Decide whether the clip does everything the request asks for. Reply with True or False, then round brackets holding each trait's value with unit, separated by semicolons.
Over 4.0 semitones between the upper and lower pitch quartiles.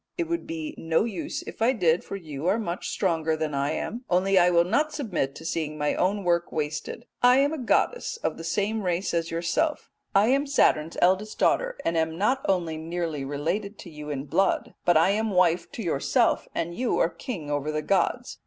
True (5.0 semitones)